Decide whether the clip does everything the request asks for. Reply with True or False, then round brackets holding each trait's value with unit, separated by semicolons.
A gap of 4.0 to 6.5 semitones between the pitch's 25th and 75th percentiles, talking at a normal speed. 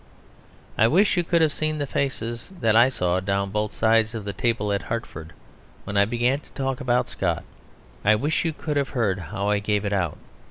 False (5.0 semitones; 210 wpm)